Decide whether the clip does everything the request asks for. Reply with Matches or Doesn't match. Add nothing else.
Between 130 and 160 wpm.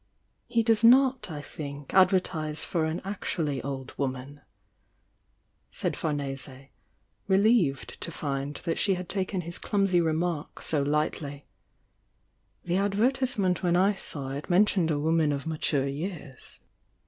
Matches